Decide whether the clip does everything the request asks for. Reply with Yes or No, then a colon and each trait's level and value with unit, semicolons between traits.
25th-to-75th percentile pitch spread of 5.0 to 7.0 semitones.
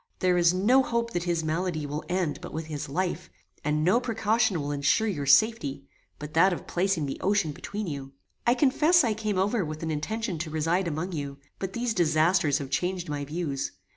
Yes: average, 5.3 semitones